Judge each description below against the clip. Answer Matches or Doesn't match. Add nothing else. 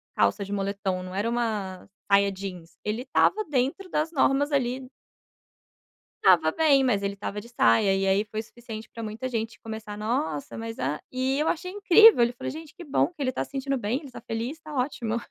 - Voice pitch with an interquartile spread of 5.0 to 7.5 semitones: Matches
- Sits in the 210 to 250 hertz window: Matches